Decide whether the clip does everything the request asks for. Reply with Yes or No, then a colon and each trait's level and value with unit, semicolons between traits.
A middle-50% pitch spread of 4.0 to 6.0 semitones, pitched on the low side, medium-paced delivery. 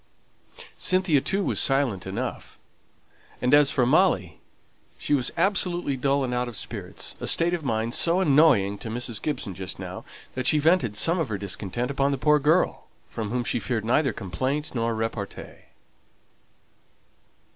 Yes: wide, 5.5 semitones; low, 130 Hz; average, 160 wpm